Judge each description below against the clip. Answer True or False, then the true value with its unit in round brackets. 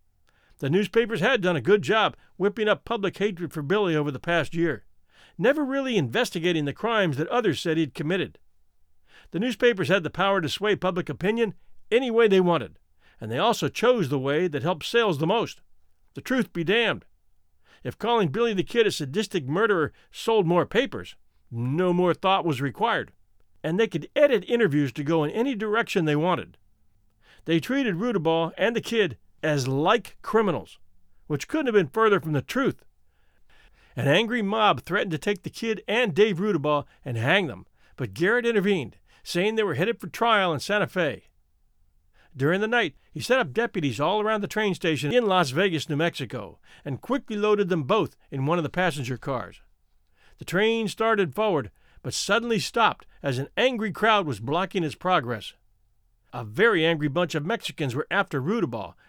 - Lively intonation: True (7.0 semitones)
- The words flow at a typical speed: True (180 wpm)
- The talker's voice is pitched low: False (175 Hz)